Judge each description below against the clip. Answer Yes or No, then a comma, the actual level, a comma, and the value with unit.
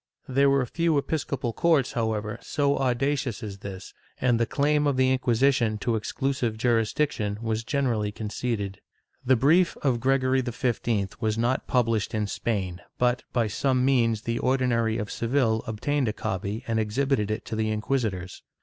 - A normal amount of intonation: Yes, average, 3.6 semitones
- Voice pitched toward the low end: Yes, low, 120 Hz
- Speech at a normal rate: Yes, average, 160 wpm